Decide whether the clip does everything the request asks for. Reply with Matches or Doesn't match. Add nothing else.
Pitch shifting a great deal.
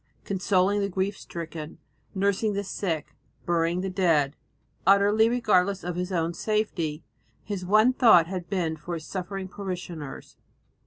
Doesn't match